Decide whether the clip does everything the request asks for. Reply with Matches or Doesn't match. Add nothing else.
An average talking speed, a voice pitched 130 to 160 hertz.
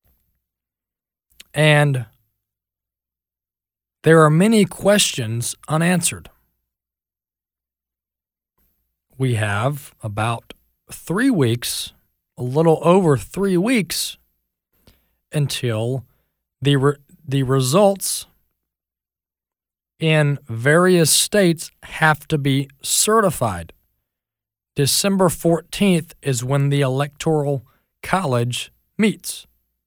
Doesn't match